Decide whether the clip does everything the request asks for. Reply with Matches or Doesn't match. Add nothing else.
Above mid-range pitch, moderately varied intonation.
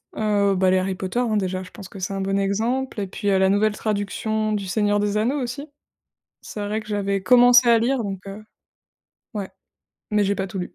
Doesn't match